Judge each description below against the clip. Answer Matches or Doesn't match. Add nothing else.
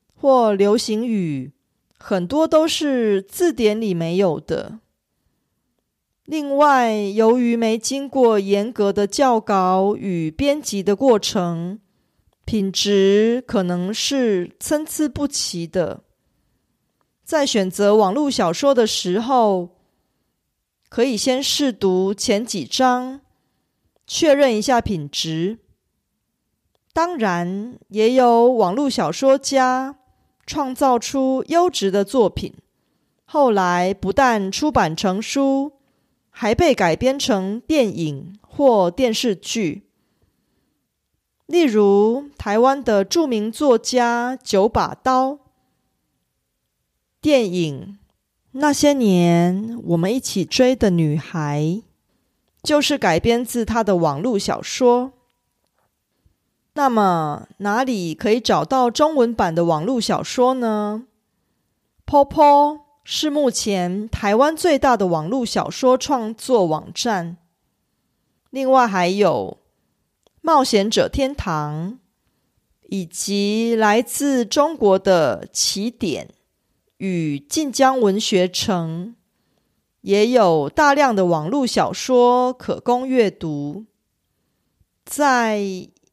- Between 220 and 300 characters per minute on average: Doesn't match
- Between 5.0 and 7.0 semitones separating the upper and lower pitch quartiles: Matches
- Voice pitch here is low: Doesn't match